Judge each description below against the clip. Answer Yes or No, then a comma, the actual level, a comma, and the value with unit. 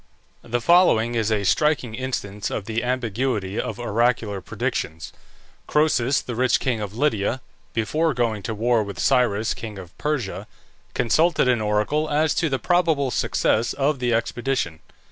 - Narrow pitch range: No, average, 4.2 semitones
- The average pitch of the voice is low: Yes, low, 120 Hz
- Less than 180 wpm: Yes, average, 150 wpm